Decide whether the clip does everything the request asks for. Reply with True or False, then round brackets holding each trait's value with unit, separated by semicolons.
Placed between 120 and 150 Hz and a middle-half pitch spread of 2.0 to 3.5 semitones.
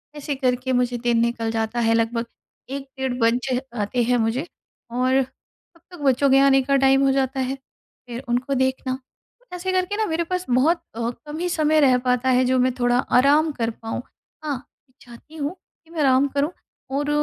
False (260 Hz; 3.0 semitones)